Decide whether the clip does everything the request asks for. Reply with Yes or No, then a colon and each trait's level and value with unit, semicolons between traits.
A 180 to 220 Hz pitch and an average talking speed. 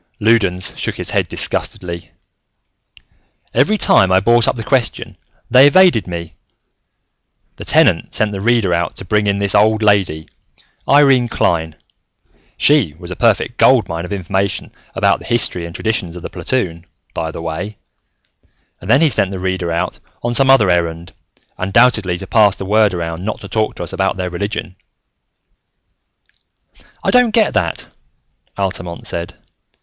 No: low, 100 Hz; average, 160 wpm